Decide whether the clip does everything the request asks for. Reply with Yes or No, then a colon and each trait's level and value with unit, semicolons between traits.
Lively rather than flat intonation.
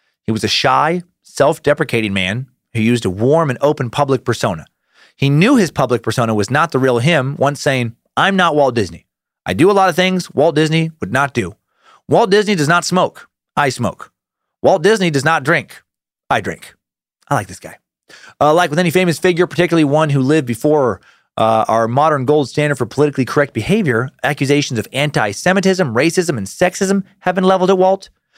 Yes: wide, 6.5 semitones